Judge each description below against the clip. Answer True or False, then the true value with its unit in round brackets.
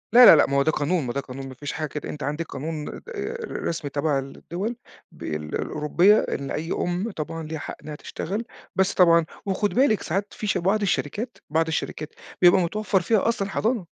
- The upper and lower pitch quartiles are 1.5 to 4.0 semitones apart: False (5.2 semitones)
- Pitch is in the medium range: True (165 Hz)